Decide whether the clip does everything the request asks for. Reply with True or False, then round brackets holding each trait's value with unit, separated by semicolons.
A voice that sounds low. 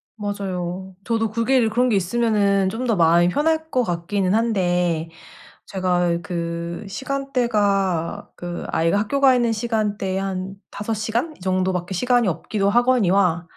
False (200 Hz)